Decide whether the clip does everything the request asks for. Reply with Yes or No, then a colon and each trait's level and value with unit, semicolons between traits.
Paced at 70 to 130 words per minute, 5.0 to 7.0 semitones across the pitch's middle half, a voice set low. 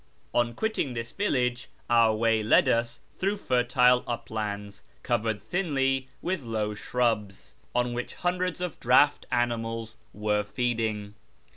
No: slow, 125 wpm; average, 2.9 semitones; low, 120 Hz